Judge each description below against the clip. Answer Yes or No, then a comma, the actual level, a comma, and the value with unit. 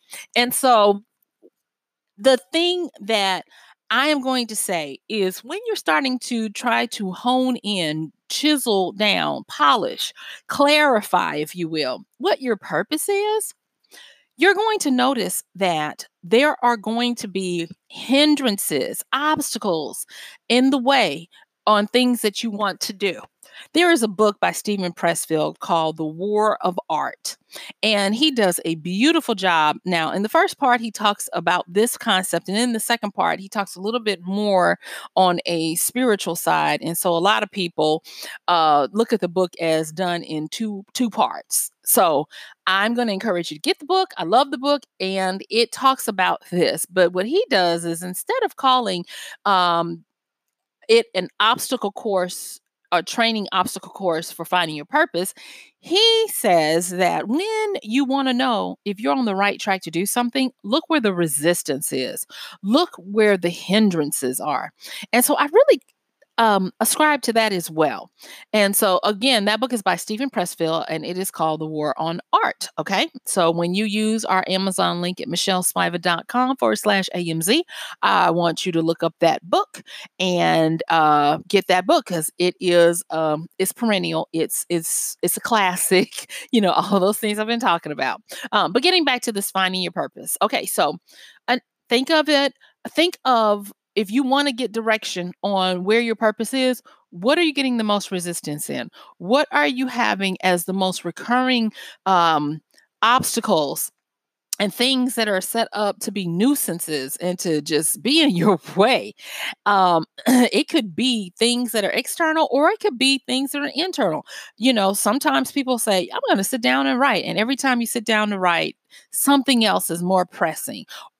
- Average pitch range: No, wide, 6.1 semitones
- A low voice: No, high, 210 Hz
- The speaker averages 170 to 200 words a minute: Yes, average, 175 wpm